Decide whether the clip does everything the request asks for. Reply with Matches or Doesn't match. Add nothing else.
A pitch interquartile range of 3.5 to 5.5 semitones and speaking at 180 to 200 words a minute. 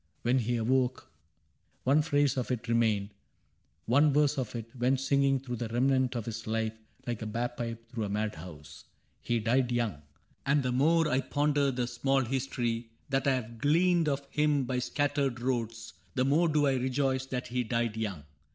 Doesn't match